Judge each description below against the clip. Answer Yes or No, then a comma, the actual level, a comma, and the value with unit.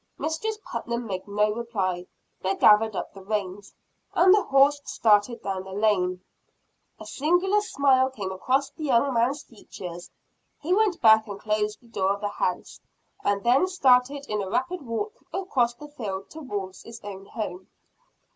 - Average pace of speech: Yes, average, 165 wpm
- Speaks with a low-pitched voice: No, high, 225 Hz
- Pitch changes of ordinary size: No, wide, 5.9 semitones